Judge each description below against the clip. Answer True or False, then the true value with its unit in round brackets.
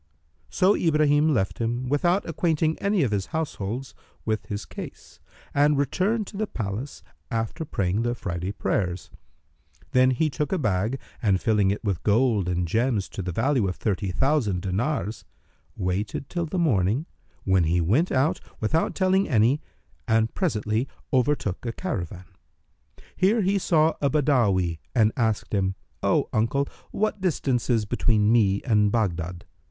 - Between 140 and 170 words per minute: True (150 wpm)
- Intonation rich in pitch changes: True (7.1 semitones)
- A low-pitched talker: True (115 Hz)